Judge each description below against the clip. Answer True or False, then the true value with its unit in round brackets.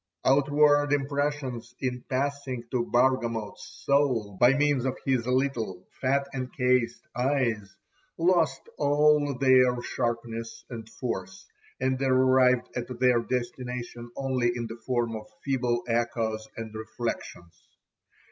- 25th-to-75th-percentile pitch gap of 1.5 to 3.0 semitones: True (2.5 semitones)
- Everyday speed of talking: False (115 wpm)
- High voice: False (125 Hz)